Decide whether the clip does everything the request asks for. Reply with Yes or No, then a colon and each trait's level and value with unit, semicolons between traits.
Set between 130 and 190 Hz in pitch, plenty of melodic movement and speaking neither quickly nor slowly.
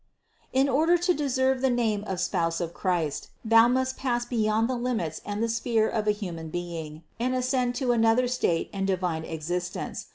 No: high, 225 Hz; wide, 6.2 semitones; average, 185 wpm